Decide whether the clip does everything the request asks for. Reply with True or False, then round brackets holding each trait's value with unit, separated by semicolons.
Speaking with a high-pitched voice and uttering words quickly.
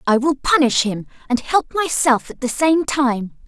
False (270 Hz; 190 wpm)